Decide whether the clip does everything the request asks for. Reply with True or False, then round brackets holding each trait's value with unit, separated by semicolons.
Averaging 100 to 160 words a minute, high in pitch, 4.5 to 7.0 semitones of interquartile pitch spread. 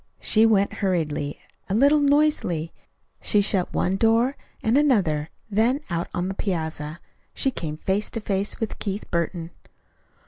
True (145 wpm; 195 Hz; 5.1 semitones)